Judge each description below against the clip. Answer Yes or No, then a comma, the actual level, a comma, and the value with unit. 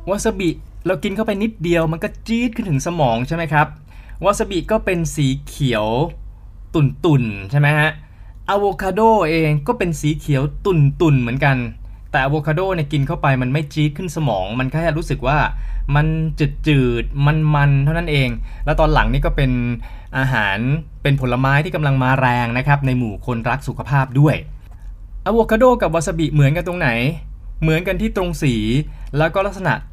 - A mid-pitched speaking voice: Yes, medium, 150 Hz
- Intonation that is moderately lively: Yes, average, 4.8 semitones